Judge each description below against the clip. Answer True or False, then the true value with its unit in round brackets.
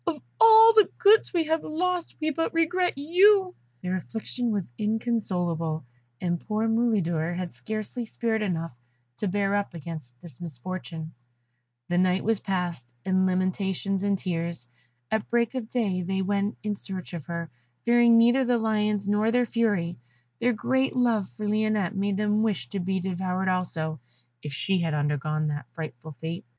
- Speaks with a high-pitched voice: True (200 Hz)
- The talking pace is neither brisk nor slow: True (160 wpm)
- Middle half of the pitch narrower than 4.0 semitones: False (5.1 semitones)